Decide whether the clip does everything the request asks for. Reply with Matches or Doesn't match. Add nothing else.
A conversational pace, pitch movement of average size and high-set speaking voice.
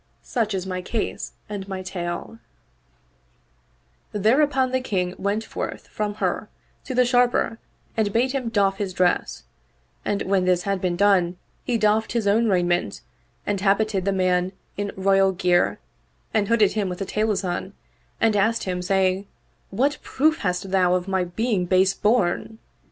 Matches